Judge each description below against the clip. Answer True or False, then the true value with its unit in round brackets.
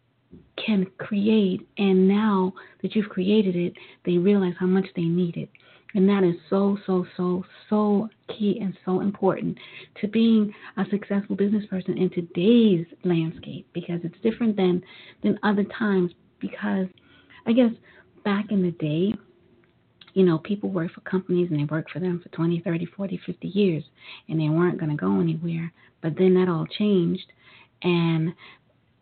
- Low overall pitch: False (185 Hz)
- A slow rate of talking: False (165 wpm)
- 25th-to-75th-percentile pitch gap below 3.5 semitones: True (2.8 semitones)